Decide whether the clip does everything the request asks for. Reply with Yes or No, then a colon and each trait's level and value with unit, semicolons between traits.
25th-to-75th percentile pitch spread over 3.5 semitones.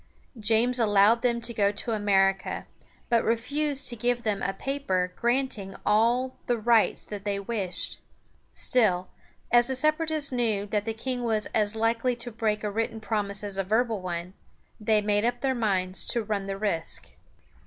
No: average, 3.0 semitones